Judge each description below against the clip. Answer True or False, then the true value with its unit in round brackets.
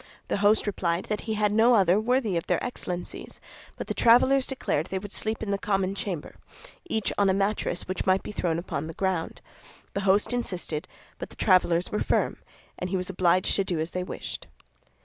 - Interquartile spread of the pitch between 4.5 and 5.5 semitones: False (3.0 semitones)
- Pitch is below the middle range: False (195 Hz)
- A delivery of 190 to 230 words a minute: True (205 wpm)